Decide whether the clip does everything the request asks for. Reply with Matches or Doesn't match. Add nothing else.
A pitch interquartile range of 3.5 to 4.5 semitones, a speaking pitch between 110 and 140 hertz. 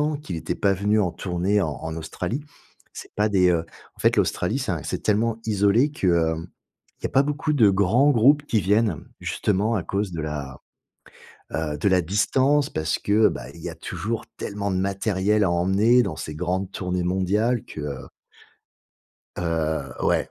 Doesn't match